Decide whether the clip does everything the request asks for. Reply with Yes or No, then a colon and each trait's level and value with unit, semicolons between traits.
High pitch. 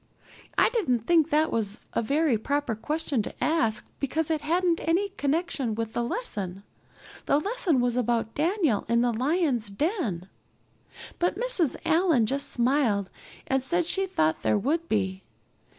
Yes: very high, 280 Hz